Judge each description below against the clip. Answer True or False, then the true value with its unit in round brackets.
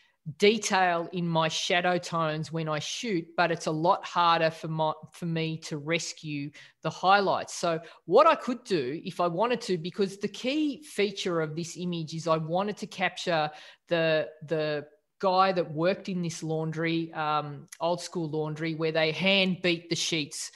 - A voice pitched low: False (170 Hz)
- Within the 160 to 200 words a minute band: True (175 wpm)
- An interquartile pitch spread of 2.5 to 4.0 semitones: True (2.8 semitones)